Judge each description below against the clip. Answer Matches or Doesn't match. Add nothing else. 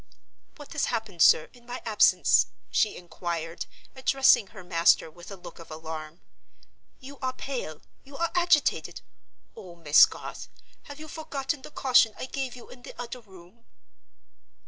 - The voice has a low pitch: Doesn't match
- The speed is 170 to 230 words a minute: Doesn't match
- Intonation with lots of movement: Matches